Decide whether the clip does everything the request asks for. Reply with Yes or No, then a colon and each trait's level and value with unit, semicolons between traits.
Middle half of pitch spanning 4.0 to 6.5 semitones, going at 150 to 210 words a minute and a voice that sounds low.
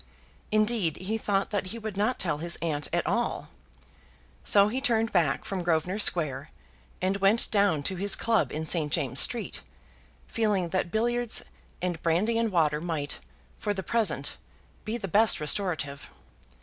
No: average, 5.0 semitones; average, 160 wpm; high, 190 Hz